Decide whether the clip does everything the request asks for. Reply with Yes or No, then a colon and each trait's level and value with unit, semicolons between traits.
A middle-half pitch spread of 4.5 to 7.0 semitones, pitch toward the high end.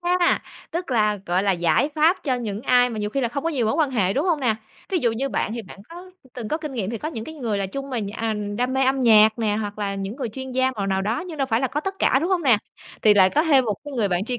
Yes: average, 4.8 semitones; high, 245 Hz